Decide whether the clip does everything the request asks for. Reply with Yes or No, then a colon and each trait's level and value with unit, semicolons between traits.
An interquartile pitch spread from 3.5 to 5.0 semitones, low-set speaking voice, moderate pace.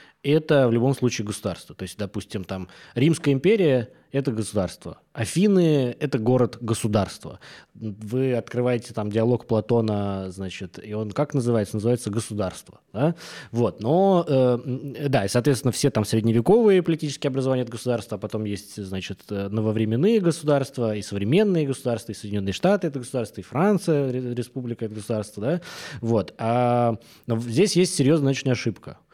Yes: average, 4.6 semitones; low, 120 Hz; average, 145 wpm